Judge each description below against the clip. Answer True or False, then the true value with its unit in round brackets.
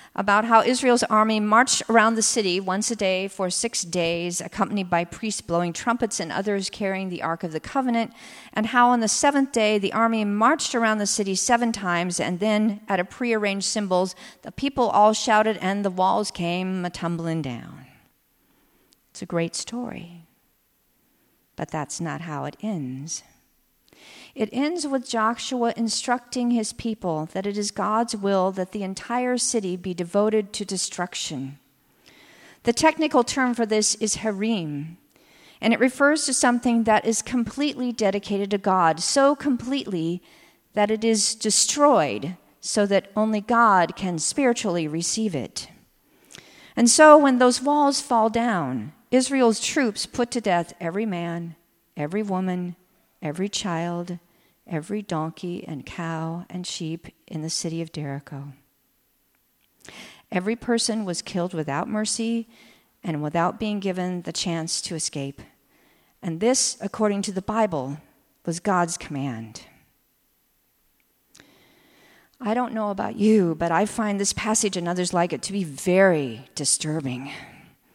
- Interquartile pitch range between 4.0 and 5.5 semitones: True (4.9 semitones)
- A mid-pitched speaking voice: False (205 Hz)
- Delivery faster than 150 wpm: False (145 wpm)